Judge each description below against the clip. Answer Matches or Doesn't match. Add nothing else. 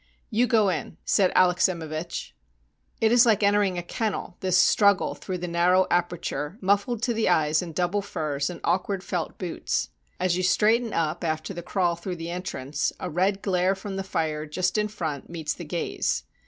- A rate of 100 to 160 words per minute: Doesn't match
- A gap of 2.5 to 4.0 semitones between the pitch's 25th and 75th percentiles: Matches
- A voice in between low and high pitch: Matches